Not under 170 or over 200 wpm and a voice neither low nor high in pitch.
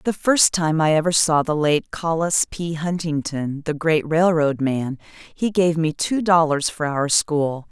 Yes: average, 180 wpm; medium, 160 Hz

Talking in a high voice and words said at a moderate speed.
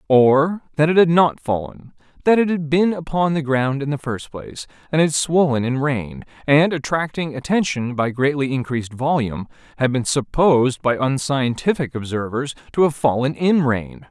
No: medium, 140 Hz; average, 170 wpm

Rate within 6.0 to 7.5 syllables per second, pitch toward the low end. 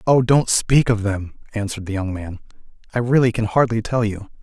No: 5.5 syllables/s; low, 110 Hz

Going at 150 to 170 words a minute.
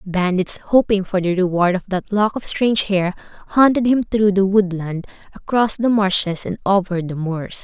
No: average, 180 wpm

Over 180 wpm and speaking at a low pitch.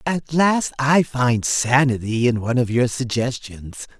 No: average, 150 wpm; low, 130 Hz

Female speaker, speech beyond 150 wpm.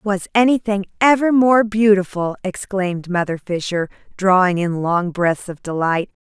No: female; slow, 135 wpm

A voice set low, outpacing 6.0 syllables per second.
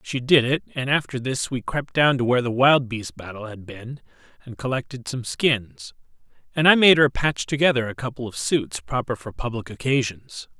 No: low, 125 Hz; 5.1 syllables/s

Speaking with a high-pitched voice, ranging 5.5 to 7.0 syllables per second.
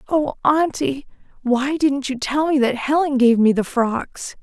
No: very high, 270 Hz; 4.0 syllables/s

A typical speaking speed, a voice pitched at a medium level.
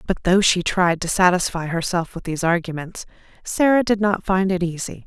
Yes: average, 190 wpm; medium, 180 Hz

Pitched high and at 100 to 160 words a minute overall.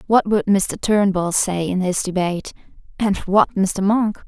Yes: high, 195 Hz; average, 155 wpm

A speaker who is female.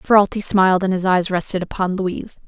Yes: female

